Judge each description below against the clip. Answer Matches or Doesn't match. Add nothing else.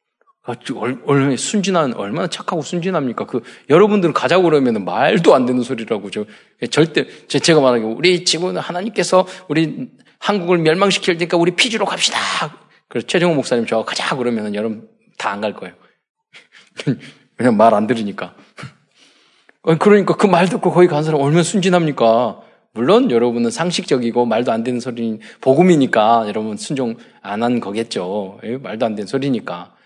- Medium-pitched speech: Matches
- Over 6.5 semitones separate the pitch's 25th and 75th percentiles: Matches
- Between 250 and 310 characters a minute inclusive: Doesn't match